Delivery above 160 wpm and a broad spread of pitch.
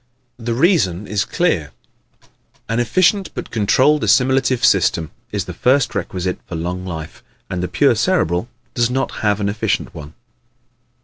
No: average, 145 wpm; wide, 6.2 semitones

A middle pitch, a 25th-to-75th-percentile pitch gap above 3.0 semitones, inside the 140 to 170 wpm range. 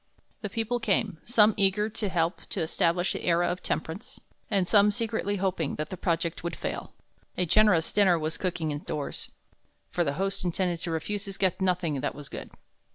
No: medium, 180 Hz; average, 3.6 semitones; average, 185 wpm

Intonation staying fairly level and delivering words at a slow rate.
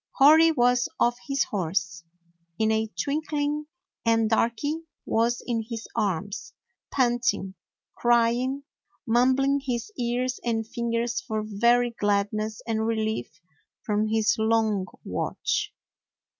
Yes: narrow, 2.3 semitones; slow, 115 wpm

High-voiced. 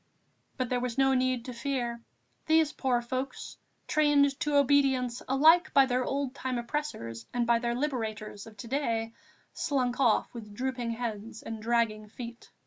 Yes: high, 245 Hz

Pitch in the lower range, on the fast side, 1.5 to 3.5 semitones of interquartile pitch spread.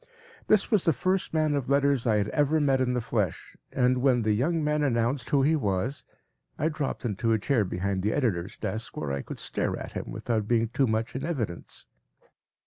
No: low, 125 Hz; fast, 210 wpm; average, 4.9 semitones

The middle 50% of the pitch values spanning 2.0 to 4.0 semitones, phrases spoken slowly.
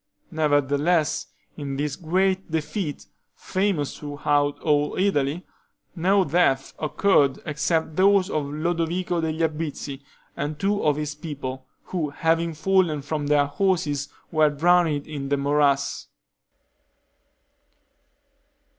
Yes: average, 3.2 semitones; slow, 110 wpm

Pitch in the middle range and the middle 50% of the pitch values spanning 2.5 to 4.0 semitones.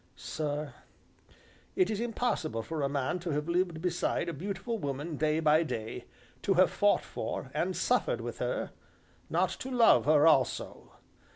No: medium, 165 Hz; average, 4.5 semitones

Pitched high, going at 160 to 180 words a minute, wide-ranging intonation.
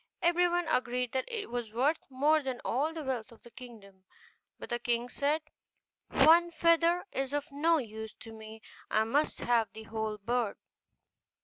Yes: very high, 250 Hz; average, 170 wpm; wide, 5.7 semitones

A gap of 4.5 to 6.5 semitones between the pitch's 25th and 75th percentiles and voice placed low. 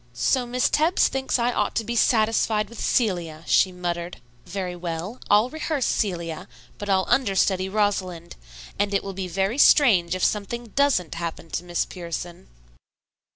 No: average, 5.0 semitones; high, 195 Hz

